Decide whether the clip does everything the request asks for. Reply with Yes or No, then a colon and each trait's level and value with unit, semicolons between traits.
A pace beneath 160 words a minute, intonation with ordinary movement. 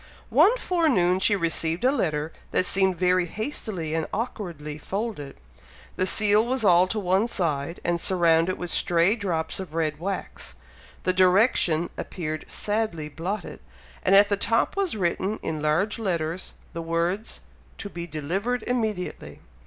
Yes: average, 145 wpm; average, 4.1 semitones